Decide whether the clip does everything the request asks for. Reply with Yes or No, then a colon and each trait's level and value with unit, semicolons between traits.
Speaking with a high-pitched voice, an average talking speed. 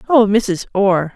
Yes: high, 205 Hz; average, 155 wpm